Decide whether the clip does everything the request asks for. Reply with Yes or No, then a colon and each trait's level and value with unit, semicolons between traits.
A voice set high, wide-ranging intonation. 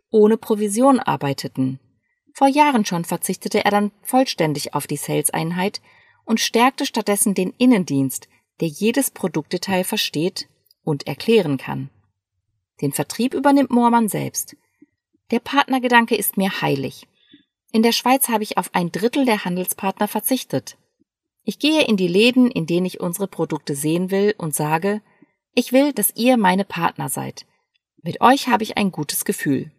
Yes: high, 205 Hz; wide, 6.8 semitones